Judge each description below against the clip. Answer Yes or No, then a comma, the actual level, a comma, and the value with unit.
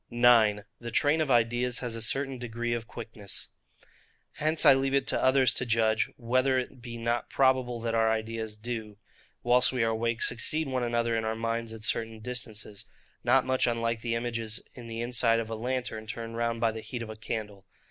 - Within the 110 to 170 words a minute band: No, average, 200 wpm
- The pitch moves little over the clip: Yes, narrow, 1.7 semitones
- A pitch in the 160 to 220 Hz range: No, low, 115 Hz